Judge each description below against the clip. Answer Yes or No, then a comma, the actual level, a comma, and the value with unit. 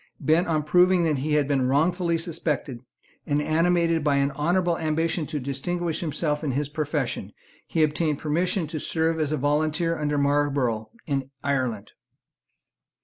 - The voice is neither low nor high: Yes, medium, 155 Hz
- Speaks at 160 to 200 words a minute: No, average, 150 wpm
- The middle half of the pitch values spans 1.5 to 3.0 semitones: Yes, narrow, 2.6 semitones